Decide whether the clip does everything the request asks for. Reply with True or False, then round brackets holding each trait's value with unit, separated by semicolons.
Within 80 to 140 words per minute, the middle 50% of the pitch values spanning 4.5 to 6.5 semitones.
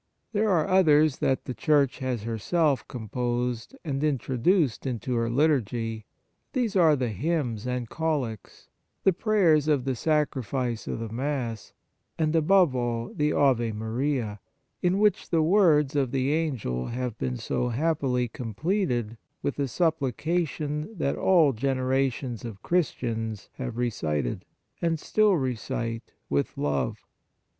True (135 wpm; 5.1 semitones)